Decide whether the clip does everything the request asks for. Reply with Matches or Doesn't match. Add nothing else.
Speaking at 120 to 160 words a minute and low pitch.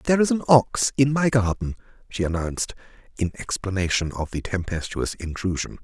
Matches